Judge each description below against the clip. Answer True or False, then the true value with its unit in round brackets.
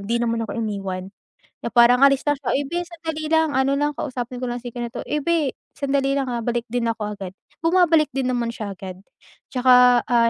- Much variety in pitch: False (3.3 semitones)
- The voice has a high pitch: True (245 Hz)